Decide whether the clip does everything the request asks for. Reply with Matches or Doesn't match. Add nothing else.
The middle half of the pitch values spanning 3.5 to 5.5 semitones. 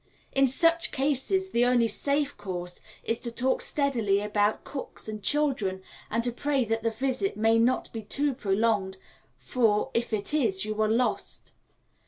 Matches